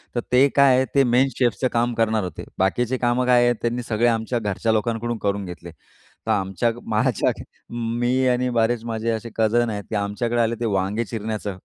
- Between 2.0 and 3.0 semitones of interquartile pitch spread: Yes, narrow, 2.4 semitones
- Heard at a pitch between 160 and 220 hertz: No, low, 115 Hz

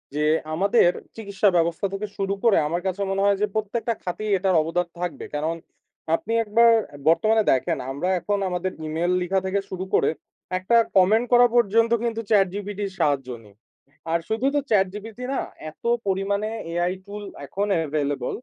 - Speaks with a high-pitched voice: Yes, high, 195 Hz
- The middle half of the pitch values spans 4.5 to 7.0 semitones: No, average, 3.5 semitones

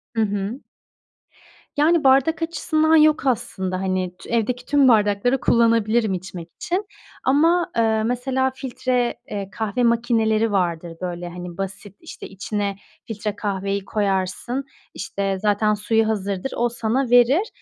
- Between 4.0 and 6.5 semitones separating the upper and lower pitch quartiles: Yes, average, 4.3 semitones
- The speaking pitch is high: Yes, high, 220 Hz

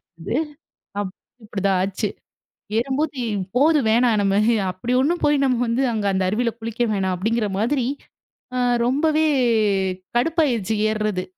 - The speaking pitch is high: Yes, high, 230 Hz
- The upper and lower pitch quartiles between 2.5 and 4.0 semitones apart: No, average, 5.1 semitones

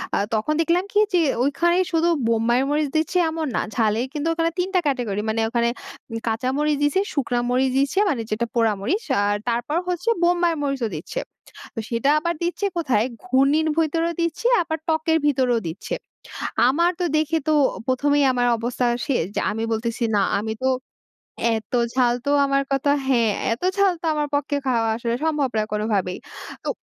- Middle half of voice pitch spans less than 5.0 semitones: No, wide, 5.6 semitones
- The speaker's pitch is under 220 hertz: No, very high, 275 Hz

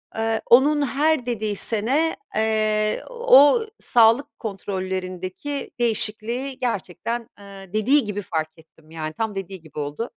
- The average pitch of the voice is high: Yes, high, 220 Hz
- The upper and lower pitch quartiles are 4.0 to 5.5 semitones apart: Yes, average, 4.8 semitones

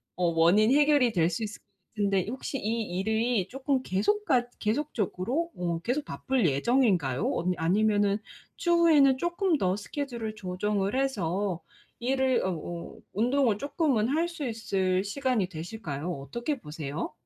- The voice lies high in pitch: Yes, high, 220 Hz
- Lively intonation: Yes, wide, 6.5 semitones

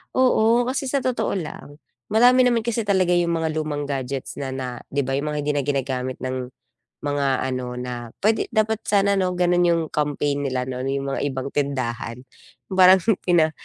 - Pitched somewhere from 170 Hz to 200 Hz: No, medium, 145 Hz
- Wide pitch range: Yes, wide, 6.4 semitones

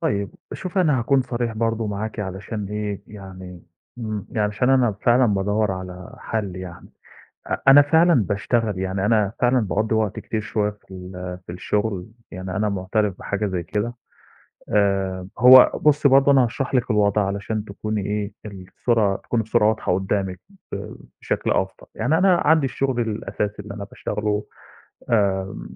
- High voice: No, low, 105 Hz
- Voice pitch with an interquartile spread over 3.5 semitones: No, average, 3.2 semitones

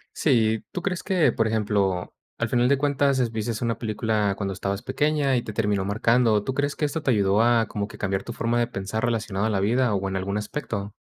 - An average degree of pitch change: Yes, average, 3.7 semitones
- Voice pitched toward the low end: Yes, low, 110 Hz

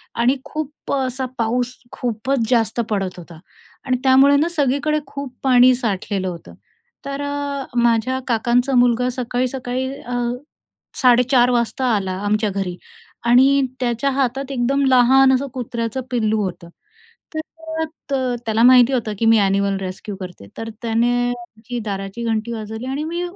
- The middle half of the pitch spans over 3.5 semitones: No, average, 3.2 semitones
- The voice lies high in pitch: Yes, high, 245 Hz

